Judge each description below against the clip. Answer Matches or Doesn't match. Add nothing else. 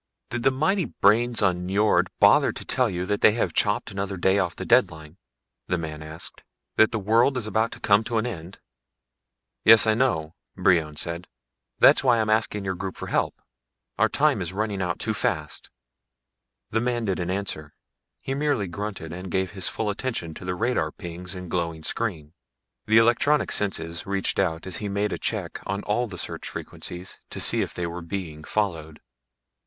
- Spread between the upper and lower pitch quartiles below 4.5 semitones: Matches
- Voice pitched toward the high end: Doesn't match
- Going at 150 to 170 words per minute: Doesn't match